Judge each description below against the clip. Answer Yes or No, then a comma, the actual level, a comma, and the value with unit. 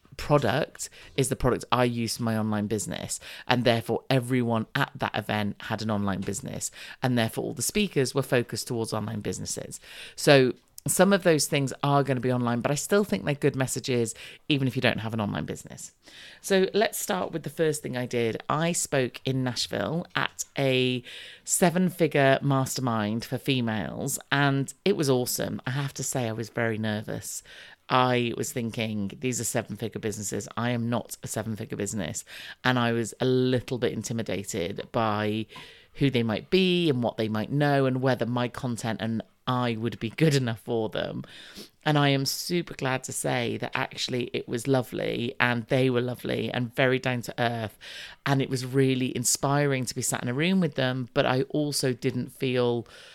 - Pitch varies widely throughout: No, average, 3.2 semitones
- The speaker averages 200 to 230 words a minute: No, average, 190 wpm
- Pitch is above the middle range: No, low, 125 Hz